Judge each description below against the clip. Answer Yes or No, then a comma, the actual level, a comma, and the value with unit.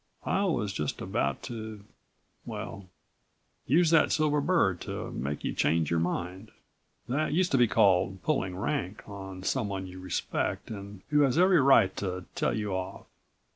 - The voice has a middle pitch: No, low, 100 Hz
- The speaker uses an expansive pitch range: Yes, wide, 7.1 semitones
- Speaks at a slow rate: No, average, 160 wpm